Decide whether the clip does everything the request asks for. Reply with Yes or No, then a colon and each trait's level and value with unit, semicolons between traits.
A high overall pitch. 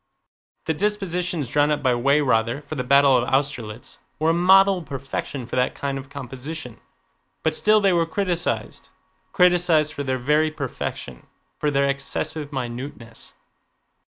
No: medium, 145 Hz